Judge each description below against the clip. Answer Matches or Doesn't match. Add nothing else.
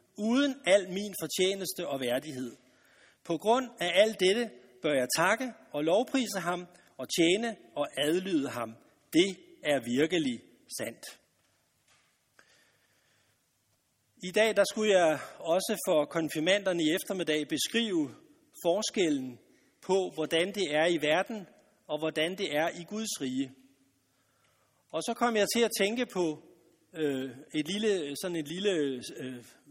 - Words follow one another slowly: Matches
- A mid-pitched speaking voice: Matches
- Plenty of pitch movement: Matches